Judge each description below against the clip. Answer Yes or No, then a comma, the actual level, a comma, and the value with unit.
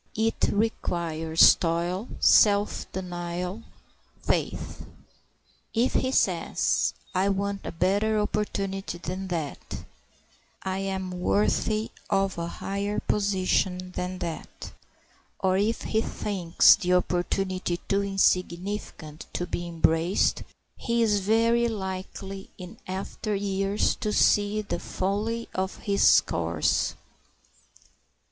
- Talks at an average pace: No, slow, 105 wpm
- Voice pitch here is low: No, high, 195 Hz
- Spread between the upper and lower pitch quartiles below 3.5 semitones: Yes, narrow, 2.4 semitones